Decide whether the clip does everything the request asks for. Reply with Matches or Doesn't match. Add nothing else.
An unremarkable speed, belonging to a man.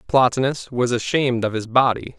Matches